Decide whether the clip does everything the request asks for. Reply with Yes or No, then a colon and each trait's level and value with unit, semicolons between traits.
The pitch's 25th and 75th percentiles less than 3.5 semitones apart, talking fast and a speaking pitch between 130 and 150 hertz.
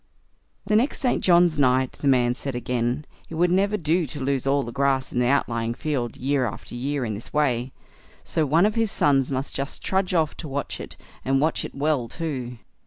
No: average, 4.2 semitones; fast, 210 wpm; medium, 140 Hz